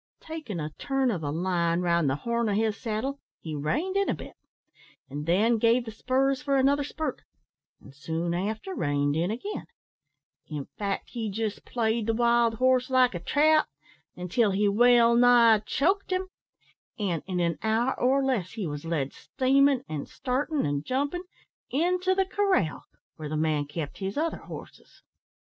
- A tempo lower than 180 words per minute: Yes, average, 170 wpm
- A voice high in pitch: Yes, high, 225 Hz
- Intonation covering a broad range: Yes, wide, 7.8 semitones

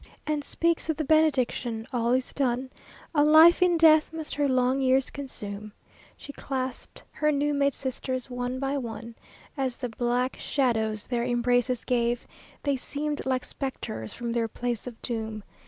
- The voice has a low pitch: No, very high, 255 Hz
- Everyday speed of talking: Yes, average, 155 wpm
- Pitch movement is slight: No, average, 3.1 semitones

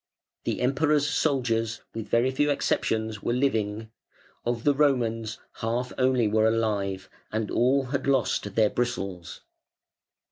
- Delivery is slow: Yes, slow, 130 wpm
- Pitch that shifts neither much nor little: Yes, average, 3.3 semitones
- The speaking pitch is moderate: No, low, 115 Hz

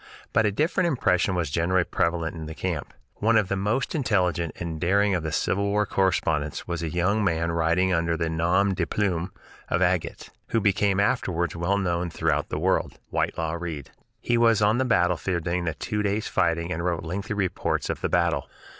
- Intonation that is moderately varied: Yes, average, 3.2 semitones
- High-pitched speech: No, very low, 90 Hz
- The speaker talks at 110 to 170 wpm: No, average, 195 wpm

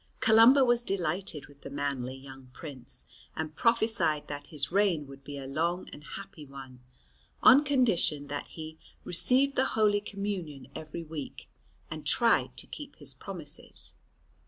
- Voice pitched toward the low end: No, medium, 160 Hz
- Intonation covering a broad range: Yes, wide, 6.4 semitones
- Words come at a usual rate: Yes, average, 150 wpm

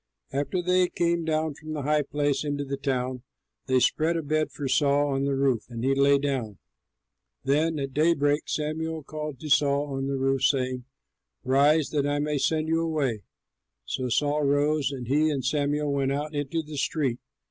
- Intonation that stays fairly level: Yes, narrow, 2.2 semitones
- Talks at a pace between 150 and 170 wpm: No, average, 185 wpm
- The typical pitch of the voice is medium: Yes, medium, 145 Hz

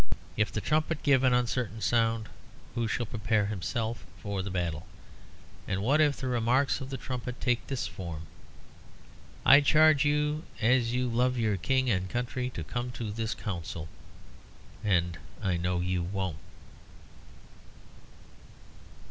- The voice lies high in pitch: No, low, 115 Hz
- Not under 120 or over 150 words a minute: Yes, average, 140 wpm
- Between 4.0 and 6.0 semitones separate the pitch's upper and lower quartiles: Yes, average, 4.9 semitones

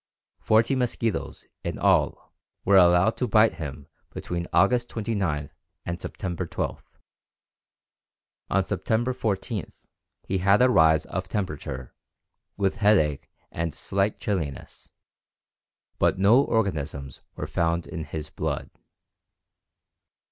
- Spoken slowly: Yes, slow, 110 wpm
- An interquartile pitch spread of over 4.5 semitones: Yes, average, 5.2 semitones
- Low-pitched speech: Yes, very low, 95 Hz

